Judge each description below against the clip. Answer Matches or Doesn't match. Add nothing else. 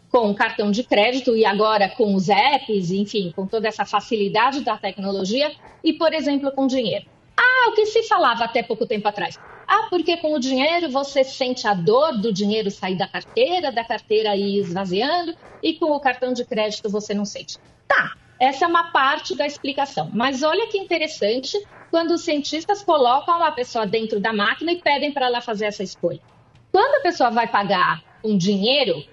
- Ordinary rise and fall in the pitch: Doesn't match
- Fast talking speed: Matches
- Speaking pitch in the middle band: Doesn't match